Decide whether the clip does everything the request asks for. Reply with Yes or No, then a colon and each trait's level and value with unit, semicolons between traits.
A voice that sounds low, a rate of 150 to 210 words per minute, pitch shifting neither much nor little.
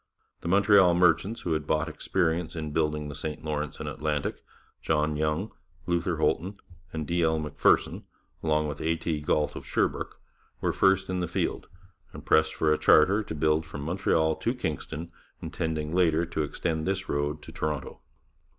No: very low, 80 Hz; average, 170 wpm; narrow, 2.2 semitones